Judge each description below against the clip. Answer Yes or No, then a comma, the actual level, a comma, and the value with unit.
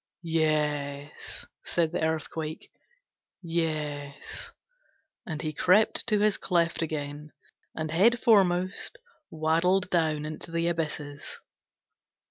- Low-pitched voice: No, medium, 160 Hz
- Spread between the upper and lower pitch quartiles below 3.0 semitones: Yes, narrow, 2.4 semitones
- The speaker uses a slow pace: Yes, slow, 95 wpm